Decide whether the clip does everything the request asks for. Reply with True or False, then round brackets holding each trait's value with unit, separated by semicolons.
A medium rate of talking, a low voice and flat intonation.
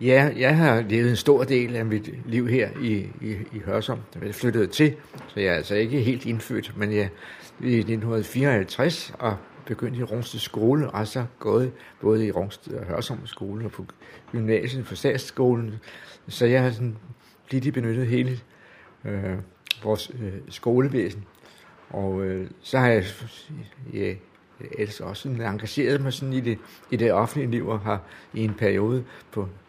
False (175 wpm; 115 Hz; 3.6 semitones)